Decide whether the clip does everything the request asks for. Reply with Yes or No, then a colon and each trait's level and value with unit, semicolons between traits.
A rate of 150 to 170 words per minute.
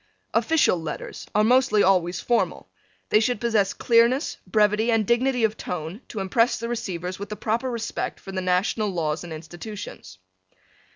Yes: average, 160 wpm